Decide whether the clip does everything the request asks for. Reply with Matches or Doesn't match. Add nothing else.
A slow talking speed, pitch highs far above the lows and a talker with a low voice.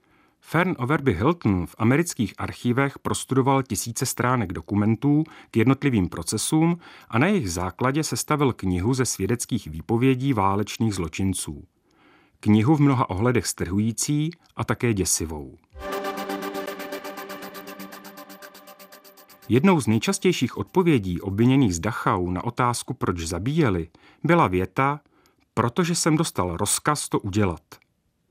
Matches